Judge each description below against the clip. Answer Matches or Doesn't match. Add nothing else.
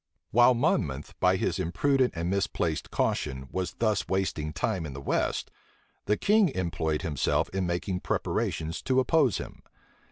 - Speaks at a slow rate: Doesn't match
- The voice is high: Doesn't match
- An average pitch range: Doesn't match